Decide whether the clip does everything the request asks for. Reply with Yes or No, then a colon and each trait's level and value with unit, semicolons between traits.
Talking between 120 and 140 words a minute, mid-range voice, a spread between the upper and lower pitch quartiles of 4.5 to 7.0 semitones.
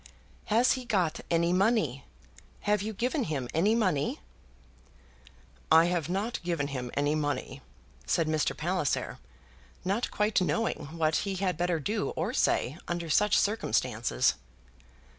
Yes: slow, 135 wpm; medium, 175 Hz; average, 5.3 semitones